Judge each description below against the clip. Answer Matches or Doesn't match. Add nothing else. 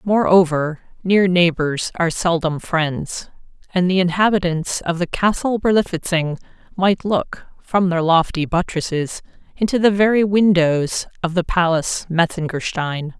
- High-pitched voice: Doesn't match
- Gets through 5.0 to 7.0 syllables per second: Doesn't match